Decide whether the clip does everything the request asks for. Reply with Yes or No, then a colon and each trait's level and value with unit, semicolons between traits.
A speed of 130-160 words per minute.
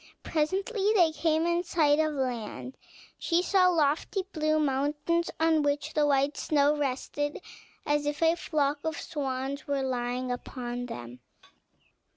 Yes: average, 140 wpm